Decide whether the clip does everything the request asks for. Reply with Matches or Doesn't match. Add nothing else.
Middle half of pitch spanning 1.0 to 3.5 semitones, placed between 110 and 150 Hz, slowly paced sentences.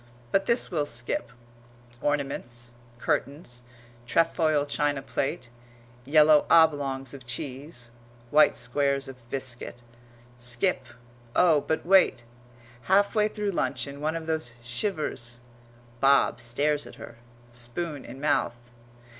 Doesn't match